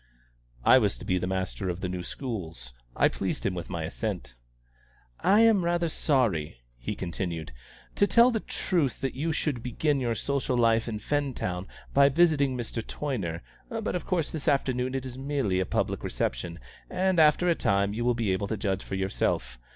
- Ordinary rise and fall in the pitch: No, wide, 7.8 semitones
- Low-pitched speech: Yes, low, 120 Hz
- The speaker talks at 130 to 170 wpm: No, average, 190 wpm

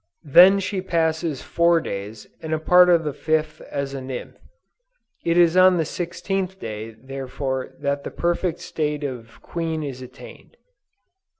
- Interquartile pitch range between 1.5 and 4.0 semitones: No, average, 4.4 semitones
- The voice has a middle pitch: Yes, medium, 155 Hz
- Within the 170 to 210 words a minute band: No, average, 155 wpm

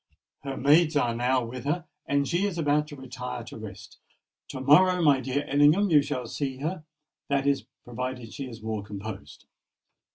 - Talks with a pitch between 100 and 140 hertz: Yes, low, 135 Hz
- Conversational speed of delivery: Yes, average, 170 wpm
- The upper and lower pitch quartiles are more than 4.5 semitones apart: No, average, 3.6 semitones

